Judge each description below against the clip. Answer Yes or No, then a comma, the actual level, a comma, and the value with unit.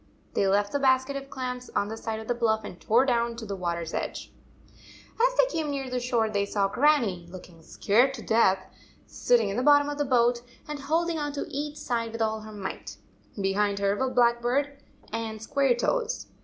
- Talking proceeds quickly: Yes, fast, 210 wpm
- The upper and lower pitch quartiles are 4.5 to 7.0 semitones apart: Yes, average, 5.0 semitones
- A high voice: Yes, high, 235 Hz